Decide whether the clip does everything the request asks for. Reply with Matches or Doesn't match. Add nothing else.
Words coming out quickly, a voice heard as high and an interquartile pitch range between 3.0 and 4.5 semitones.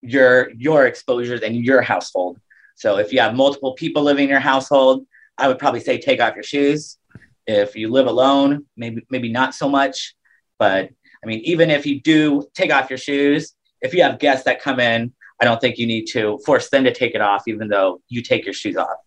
Doesn't match